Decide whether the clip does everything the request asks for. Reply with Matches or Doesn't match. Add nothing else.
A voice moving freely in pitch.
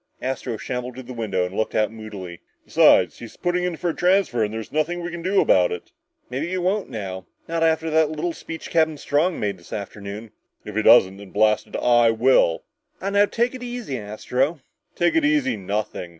Matches